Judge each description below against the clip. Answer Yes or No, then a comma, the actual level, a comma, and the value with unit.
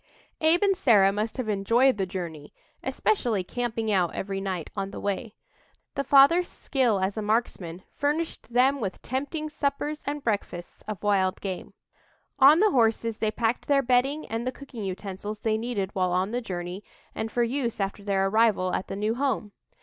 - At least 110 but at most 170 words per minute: No, average, 180 wpm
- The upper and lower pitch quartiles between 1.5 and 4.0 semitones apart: No, average, 5.3 semitones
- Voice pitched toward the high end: Yes, high, 220 Hz